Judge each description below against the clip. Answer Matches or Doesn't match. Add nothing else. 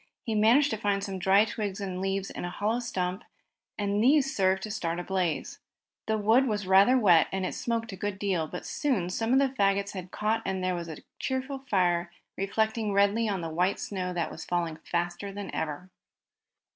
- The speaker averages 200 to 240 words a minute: Matches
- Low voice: Doesn't match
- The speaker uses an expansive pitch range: Doesn't match